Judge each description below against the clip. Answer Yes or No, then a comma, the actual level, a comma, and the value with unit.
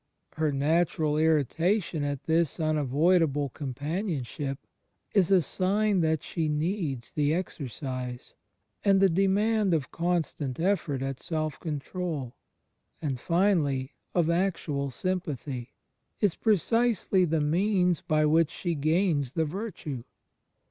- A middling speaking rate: No, slow, 115 wpm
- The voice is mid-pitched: Yes, medium, 160 Hz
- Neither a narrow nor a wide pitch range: Yes, average, 4.2 semitones